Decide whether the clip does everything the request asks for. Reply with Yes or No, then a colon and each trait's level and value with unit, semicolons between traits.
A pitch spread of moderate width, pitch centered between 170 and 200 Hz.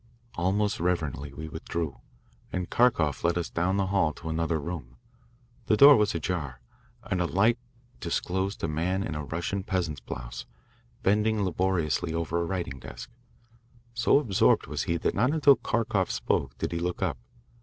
No: average, 3.8 semitones; very low, 90 Hz